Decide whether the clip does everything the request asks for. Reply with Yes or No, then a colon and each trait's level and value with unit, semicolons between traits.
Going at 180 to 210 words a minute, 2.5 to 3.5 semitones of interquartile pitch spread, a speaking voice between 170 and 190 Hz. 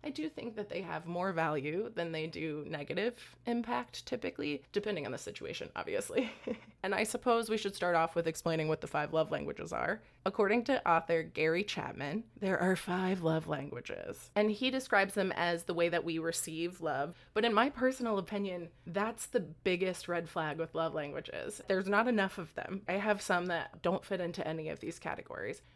No: average, 195 wpm; average, 4.7 semitones; medium, 185 Hz